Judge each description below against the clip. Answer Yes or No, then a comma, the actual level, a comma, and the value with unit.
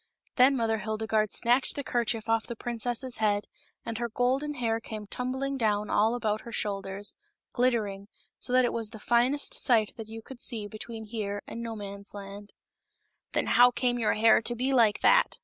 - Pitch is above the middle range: Yes, high, 225 Hz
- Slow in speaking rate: No, average, 185 wpm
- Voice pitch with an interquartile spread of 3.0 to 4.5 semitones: No, narrow, 2.5 semitones